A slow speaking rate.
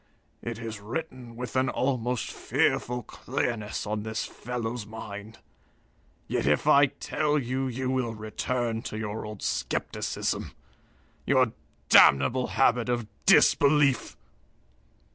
Yes: slow, 115 wpm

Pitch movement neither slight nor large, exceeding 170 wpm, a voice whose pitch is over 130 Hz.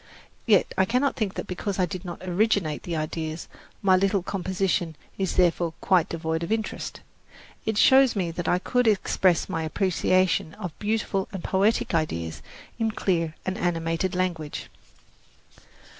No: average, 3.1 semitones; average, 150 wpm; medium, 185 Hz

